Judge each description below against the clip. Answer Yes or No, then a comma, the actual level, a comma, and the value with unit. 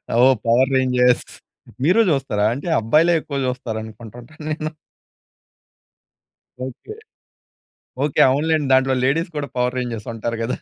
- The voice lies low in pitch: Yes, low, 130 Hz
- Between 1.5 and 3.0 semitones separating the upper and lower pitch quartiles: No, average, 3.7 semitones